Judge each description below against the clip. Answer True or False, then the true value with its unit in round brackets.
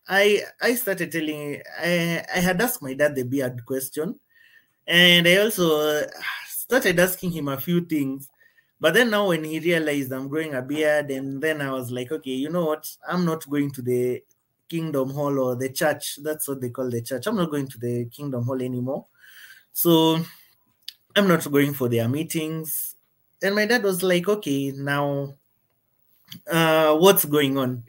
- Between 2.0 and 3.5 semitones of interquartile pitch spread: False (4.6 semitones)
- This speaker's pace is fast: False (180 wpm)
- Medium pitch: True (150 Hz)